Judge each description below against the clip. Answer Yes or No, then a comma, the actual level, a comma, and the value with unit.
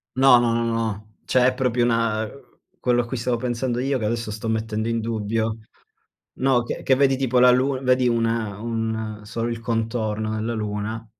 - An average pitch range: No, narrow, 2.0 semitones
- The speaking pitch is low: Yes, low, 115 Hz